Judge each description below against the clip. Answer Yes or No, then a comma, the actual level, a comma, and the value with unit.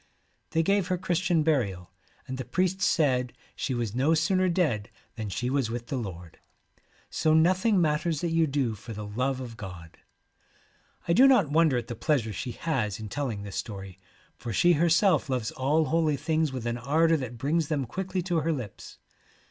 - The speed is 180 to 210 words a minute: Yes, average, 190 wpm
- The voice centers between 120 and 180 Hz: Yes, medium, 140 Hz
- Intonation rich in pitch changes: Yes, wide, 5.9 semitones